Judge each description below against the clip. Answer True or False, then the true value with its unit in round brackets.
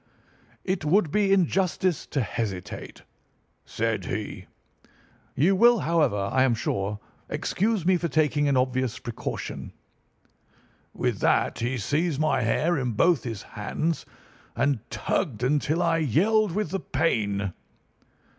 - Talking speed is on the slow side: True (125 wpm)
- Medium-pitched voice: True (150 Hz)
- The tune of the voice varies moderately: False (6.6 semitones)